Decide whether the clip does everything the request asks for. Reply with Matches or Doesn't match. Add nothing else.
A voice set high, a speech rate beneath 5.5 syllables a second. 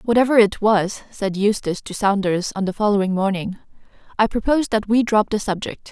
Doesn't match